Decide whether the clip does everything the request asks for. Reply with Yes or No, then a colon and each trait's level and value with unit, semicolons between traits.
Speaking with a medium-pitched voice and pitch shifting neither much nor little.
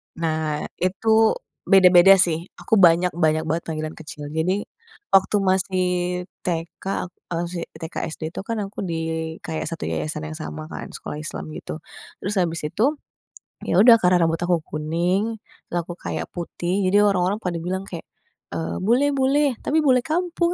Yes: medium, 180 Hz; average, 3.6 semitones